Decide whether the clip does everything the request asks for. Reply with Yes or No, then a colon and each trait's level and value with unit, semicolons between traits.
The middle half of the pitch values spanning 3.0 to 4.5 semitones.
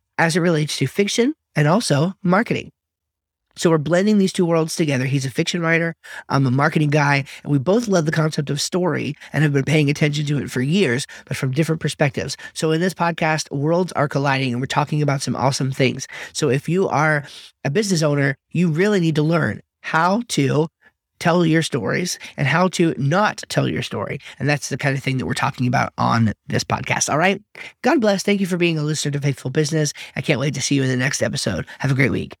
Yes: average, 3.7 semitones